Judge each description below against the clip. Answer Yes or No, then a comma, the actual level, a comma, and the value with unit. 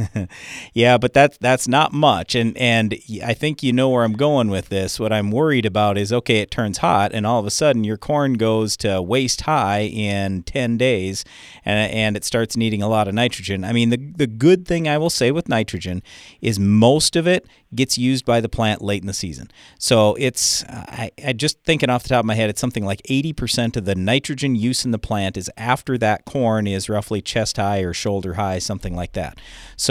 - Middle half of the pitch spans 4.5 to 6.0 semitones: No, average, 3.9 semitones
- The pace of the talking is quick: Yes, fast, 225 wpm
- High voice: No, low, 115 Hz